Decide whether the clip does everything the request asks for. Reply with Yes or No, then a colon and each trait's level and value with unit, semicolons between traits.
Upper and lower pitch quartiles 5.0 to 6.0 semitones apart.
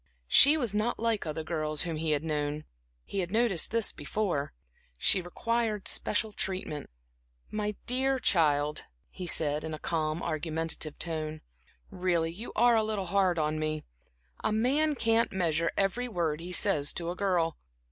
Yes: wide, 5.6 semitones